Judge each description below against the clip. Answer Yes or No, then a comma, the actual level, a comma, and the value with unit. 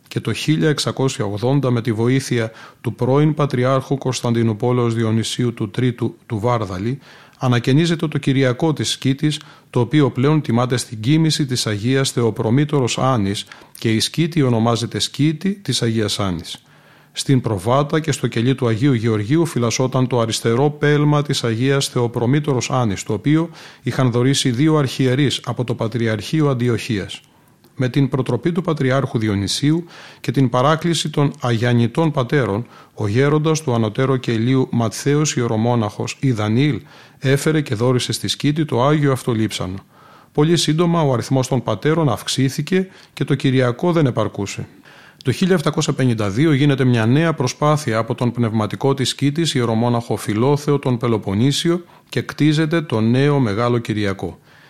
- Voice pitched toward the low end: Yes, low, 130 Hz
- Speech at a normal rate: Yes, average, 140 wpm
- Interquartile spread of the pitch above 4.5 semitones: No, average, 3.9 semitones